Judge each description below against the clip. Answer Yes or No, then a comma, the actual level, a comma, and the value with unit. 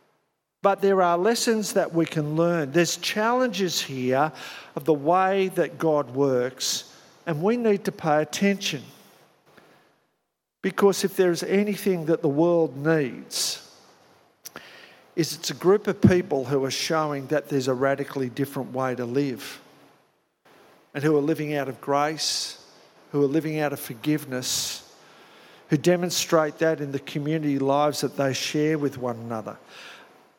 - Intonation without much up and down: No, average, 4.1 semitones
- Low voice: No, medium, 155 Hz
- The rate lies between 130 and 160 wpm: Yes, average, 145 wpm